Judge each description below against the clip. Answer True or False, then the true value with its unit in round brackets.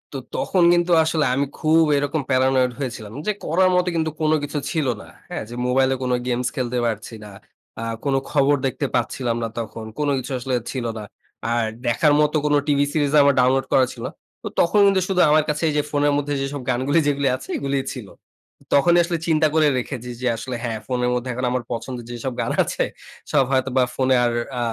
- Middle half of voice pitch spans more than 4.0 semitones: False (3.2 semitones)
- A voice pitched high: False (135 Hz)